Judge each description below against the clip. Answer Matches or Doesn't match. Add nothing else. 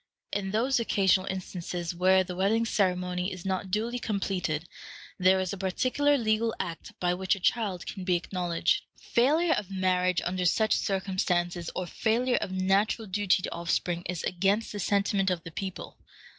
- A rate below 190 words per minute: Matches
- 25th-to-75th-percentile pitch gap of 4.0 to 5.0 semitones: Doesn't match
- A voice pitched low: Doesn't match